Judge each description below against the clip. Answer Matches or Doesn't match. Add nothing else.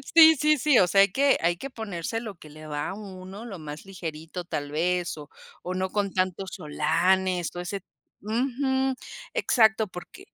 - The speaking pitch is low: Doesn't match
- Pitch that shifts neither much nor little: Matches